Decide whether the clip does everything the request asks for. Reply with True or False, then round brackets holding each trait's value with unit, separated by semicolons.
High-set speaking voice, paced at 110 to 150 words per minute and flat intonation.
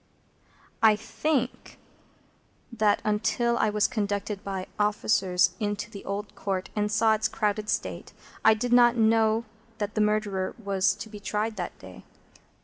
True (210 Hz; 145 wpm; 1.6 semitones)